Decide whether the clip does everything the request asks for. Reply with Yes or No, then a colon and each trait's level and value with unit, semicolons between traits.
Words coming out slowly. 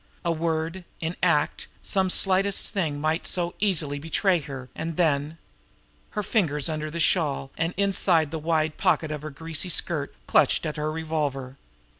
No: average, 160 wpm